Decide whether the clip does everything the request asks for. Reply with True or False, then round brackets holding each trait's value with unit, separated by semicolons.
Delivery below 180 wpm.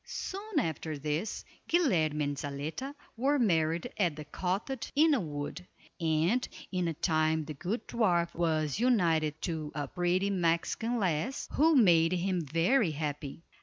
True (140 wpm)